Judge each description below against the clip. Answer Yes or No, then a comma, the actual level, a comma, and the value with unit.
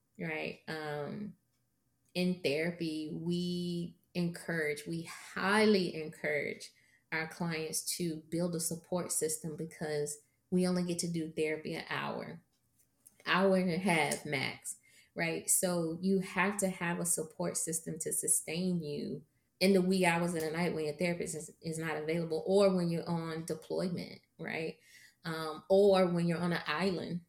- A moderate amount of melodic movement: No, narrow, 2.3 semitones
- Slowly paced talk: No, average, 150 wpm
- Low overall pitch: No, medium, 170 Hz